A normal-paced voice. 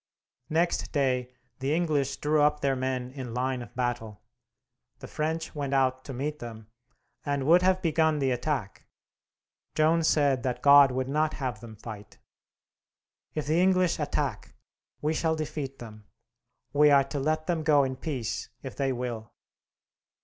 Yes: average, 155 wpm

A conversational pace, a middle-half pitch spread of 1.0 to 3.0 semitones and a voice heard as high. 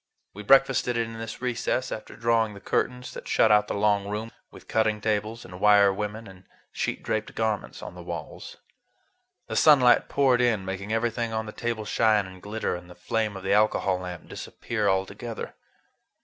No: average, 180 wpm; narrow, 2.4 semitones; low, 110 Hz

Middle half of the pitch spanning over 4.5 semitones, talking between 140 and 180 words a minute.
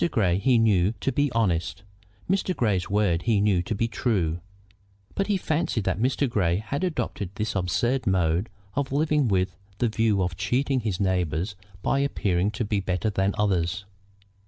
Yes: average, 5.0 semitones; average, 170 wpm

